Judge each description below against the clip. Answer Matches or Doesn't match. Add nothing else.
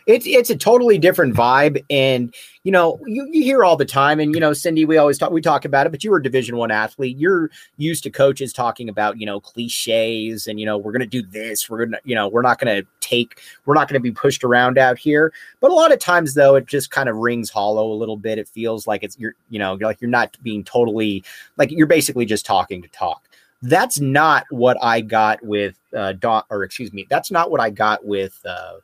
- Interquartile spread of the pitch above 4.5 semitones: Matches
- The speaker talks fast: Matches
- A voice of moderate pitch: Doesn't match